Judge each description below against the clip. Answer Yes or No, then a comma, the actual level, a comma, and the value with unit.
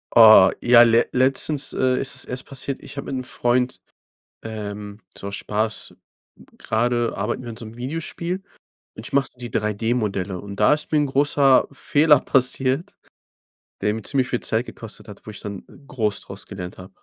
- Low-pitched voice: Yes, low, 120 Hz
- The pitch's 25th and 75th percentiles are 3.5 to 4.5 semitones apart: Yes, average, 4.0 semitones